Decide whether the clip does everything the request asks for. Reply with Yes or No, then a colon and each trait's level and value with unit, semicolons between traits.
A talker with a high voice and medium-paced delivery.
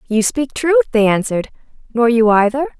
Yes: high, 230 Hz; average, 170 wpm